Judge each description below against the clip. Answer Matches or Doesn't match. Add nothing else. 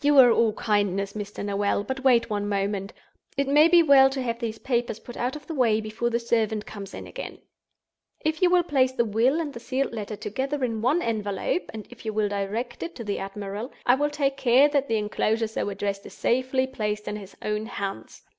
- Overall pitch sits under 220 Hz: Doesn't match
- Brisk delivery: Matches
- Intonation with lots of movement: Doesn't match